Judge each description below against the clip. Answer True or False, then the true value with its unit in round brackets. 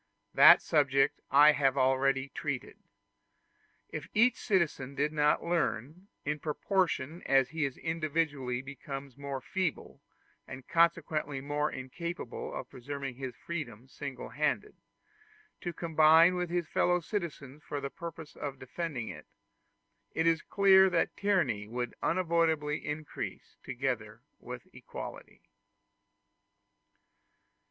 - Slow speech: True (115 wpm)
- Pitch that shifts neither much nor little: True (3.9 semitones)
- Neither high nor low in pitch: True (150 Hz)